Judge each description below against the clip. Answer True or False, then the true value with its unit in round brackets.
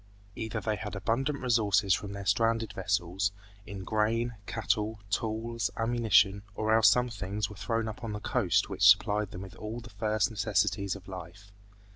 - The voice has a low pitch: True (105 Hz)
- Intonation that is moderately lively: False (2.2 semitones)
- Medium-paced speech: True (170 wpm)